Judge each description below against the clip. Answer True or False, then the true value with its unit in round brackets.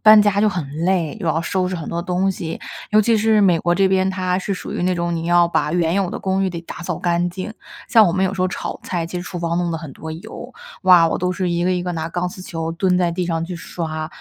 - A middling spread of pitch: False (1.9 semitones)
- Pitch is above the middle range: False (180 Hz)